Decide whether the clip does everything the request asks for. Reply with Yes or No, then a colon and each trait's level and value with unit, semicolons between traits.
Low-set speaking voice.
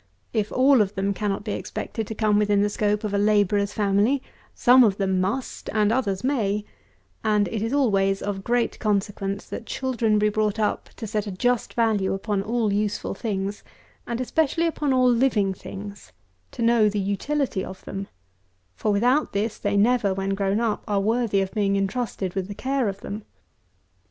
No: high, 210 Hz